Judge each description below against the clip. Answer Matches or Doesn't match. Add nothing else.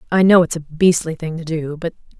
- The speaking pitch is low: Doesn't match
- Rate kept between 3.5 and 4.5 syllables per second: Doesn't match